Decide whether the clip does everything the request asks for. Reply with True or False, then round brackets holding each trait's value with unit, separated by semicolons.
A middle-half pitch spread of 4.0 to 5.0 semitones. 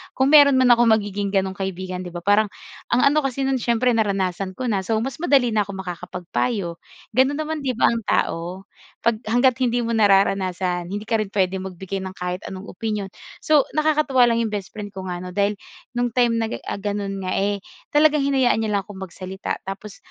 True (4.3 semitones)